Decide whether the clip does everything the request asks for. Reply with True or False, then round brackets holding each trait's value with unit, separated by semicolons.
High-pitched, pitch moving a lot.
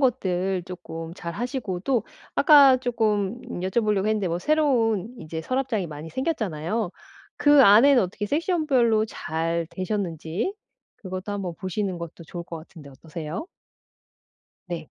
True (195 Hz; 6.3 semitones)